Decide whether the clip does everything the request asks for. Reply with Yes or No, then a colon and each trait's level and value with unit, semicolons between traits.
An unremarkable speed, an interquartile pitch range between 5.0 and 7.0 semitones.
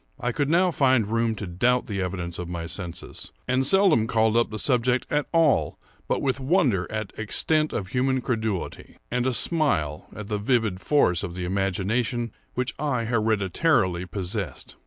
Yes: average, 170 wpm; average, 5.3 semitones